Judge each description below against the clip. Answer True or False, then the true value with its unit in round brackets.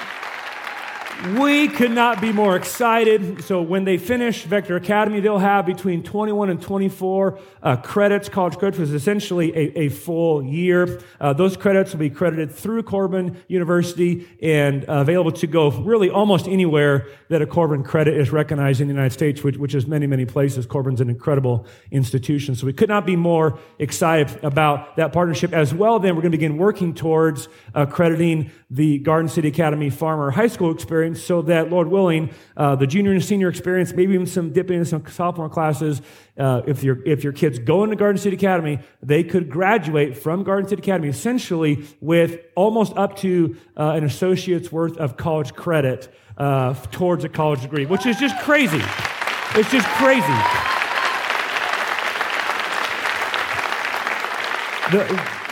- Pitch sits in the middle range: True (165 Hz)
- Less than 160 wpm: False (170 wpm)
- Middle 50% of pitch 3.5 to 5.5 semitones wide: True (4.2 semitones)